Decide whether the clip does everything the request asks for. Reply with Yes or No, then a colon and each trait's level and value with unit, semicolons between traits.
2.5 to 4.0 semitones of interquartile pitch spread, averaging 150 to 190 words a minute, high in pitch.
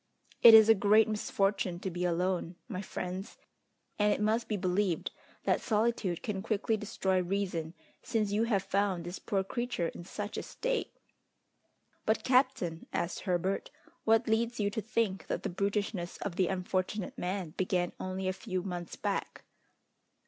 Yes: average, 3.1 semitones; average, 160 wpm; high, 195 Hz